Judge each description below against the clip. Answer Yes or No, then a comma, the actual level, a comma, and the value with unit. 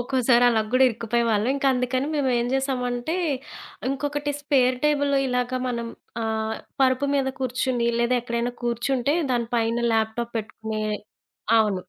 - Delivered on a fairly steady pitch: Yes, narrow, 2.3 semitones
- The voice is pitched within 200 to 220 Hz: No, high, 245 Hz